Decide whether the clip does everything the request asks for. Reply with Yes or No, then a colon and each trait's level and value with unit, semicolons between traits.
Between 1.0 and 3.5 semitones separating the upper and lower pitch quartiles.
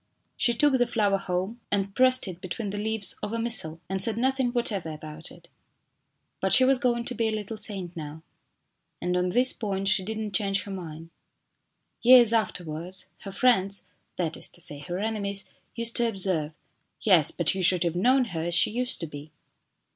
No: average, 4.6 semitones